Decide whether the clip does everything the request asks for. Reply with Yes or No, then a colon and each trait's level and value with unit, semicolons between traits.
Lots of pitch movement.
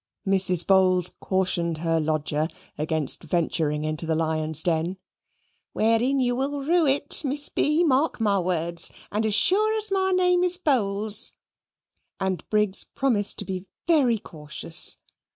Yes: wide, 8.8 semitones